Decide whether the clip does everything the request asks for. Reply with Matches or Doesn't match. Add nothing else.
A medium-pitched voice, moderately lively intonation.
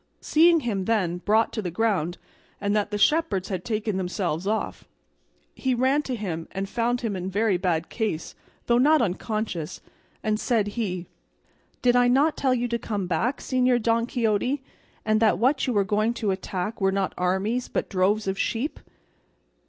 Doesn't match